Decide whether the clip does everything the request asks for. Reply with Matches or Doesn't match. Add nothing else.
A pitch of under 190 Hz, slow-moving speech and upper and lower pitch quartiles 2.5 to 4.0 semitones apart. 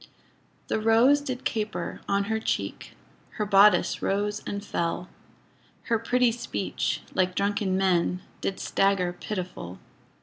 Doesn't match